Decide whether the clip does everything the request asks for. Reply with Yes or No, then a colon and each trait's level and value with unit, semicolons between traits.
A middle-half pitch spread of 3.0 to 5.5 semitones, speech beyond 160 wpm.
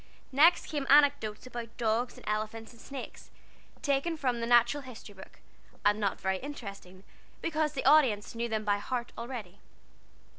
No: average, 4.6 semitones; average, 155 wpm